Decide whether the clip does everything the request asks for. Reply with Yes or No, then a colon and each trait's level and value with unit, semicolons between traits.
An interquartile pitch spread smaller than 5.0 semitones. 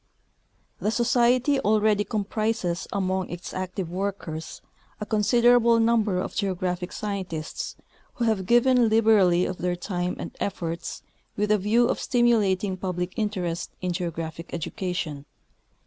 Yes: average, 3.9 semitones